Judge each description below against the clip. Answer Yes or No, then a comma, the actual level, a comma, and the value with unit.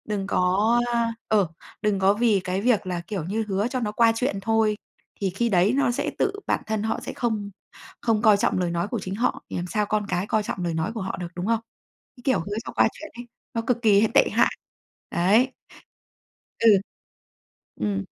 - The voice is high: Yes, high, 210 Hz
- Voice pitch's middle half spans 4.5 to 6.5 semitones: No, average, 3.2 semitones